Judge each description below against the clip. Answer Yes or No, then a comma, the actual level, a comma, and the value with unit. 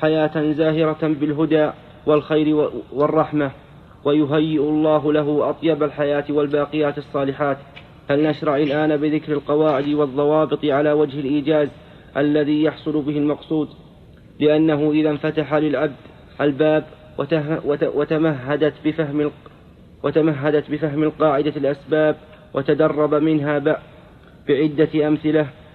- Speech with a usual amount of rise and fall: No, narrow, 0.9 semitones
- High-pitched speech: No, medium, 150 Hz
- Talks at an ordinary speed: Yes, average, 85 wpm